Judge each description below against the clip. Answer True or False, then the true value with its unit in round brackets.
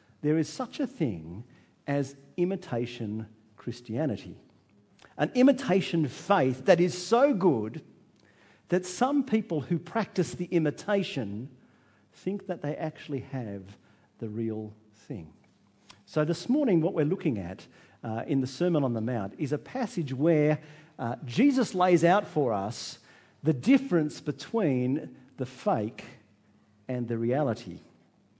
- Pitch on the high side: False (150 Hz)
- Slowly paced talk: True (125 wpm)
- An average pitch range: False (7.2 semitones)